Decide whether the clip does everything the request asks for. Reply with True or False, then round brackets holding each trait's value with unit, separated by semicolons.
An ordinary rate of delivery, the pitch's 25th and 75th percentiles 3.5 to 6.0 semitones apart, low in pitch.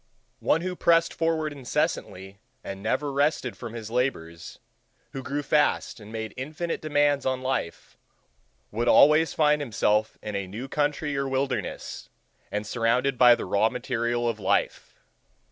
True (145 wpm; 4.8 semitones; 130 Hz)